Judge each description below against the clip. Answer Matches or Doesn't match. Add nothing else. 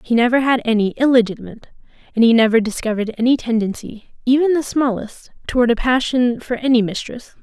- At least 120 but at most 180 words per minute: Matches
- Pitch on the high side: Matches